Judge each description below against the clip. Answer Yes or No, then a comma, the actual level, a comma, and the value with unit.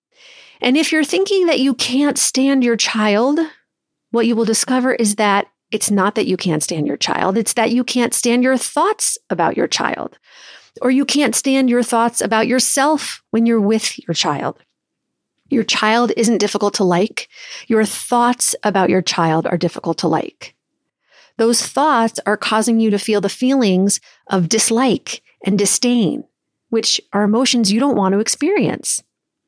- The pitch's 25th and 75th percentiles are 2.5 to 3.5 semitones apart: No, average, 3.9 semitones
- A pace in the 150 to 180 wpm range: Yes, average, 170 wpm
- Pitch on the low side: No, high, 230 Hz